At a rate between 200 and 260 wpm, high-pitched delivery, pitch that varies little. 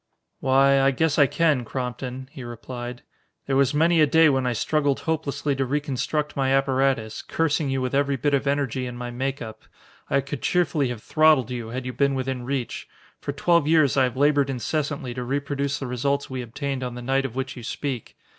No: fast, 205 wpm; low, 135 Hz; narrow, 2.2 semitones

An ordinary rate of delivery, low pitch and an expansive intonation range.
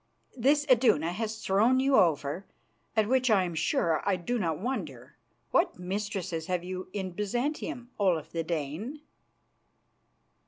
No: average, 145 wpm; high, 195 Hz; wide, 6.1 semitones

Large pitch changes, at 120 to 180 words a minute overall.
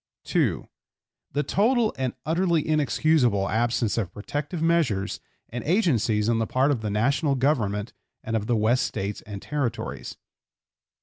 Yes: wide, 6.1 semitones; average, 140 wpm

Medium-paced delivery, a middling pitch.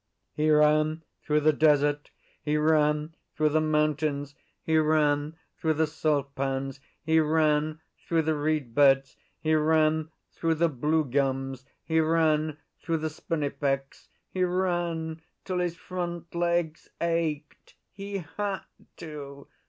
No: slow, 130 wpm; medium, 155 Hz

